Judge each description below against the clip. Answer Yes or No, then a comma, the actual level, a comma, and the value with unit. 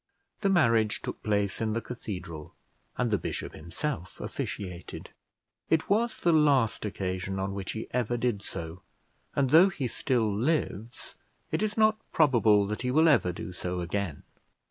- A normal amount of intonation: No, wide, 7.0 semitones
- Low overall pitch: Yes, low, 110 Hz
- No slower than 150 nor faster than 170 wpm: Yes, average, 160 wpm